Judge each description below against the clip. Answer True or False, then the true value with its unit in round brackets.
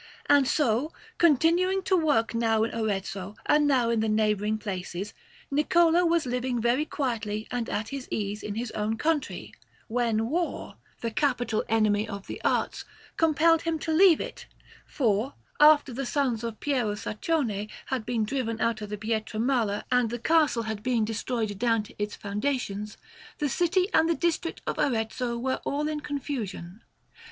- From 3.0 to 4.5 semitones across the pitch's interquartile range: False (5.4 semitones)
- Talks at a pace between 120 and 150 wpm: False (165 wpm)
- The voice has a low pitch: False (235 Hz)